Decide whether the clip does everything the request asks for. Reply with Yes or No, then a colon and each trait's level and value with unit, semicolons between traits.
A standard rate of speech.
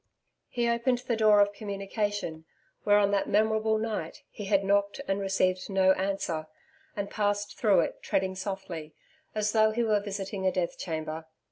Yes: average, 165 wpm